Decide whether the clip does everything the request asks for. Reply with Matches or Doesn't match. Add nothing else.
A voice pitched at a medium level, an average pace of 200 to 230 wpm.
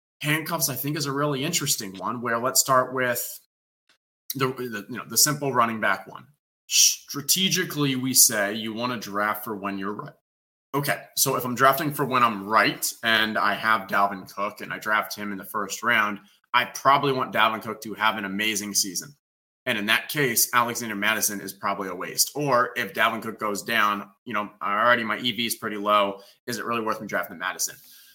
Doesn't match